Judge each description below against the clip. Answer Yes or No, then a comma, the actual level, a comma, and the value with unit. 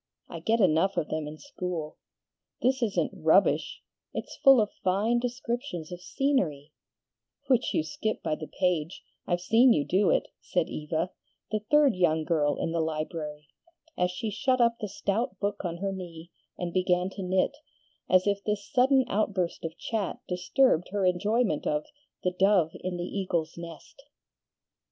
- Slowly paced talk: No, average, 165 wpm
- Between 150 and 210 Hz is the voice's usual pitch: Yes, medium, 185 Hz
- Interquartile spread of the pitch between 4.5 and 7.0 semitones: Yes, average, 5.1 semitones